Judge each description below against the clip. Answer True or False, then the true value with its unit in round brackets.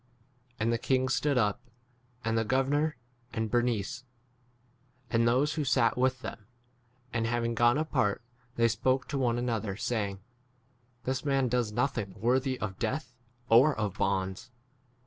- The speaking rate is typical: True (155 wpm)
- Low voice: True (120 Hz)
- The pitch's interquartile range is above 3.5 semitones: False (2.8 semitones)